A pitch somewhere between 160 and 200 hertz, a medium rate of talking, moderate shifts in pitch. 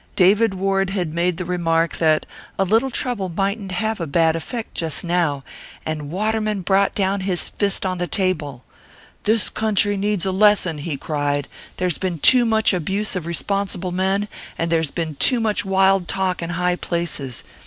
Yes: medium, 185 Hz; average, 175 wpm; average, 3.3 semitones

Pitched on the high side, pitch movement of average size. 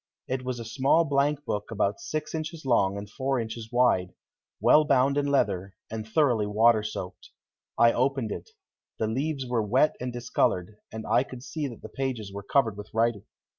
No: low, 120 Hz; average, 4.2 semitones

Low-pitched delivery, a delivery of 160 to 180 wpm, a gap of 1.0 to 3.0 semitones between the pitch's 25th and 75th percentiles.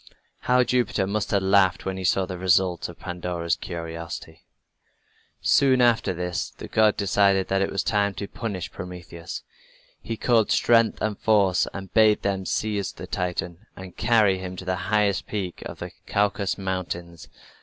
Yes: very low, 95 Hz; average, 165 wpm; average, 2.7 semitones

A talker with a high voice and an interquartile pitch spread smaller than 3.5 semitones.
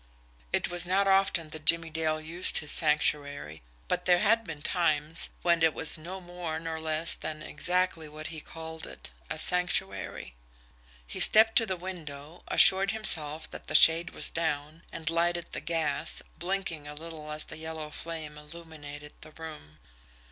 No: medium, 160 Hz; narrow, 2.4 semitones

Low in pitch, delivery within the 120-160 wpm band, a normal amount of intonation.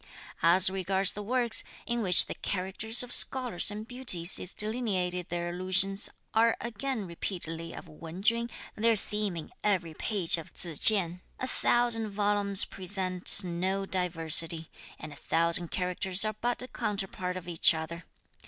No: high, 190 Hz; average, 155 wpm; average, 3.7 semitones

